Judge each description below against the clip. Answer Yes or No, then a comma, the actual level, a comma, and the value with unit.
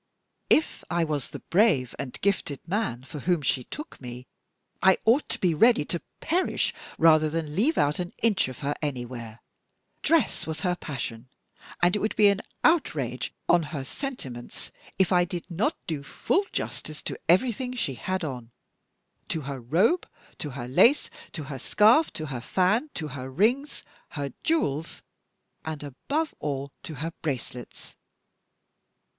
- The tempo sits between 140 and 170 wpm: Yes, average, 160 wpm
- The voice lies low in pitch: No, medium, 160 Hz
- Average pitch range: No, wide, 7.4 semitones